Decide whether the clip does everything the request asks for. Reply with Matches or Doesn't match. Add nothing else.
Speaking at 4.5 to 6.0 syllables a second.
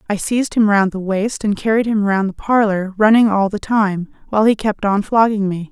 Matches